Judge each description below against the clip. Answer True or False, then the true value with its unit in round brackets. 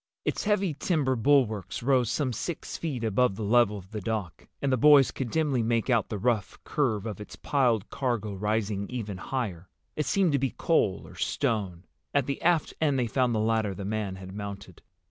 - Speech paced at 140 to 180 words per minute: False (200 wpm)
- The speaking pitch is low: True (115 Hz)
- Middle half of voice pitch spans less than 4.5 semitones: False (4.9 semitones)